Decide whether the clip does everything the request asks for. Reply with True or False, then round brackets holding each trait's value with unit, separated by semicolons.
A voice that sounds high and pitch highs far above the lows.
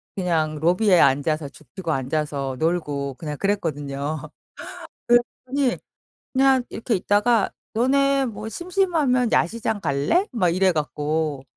False (180 Hz; 8.2 semitones)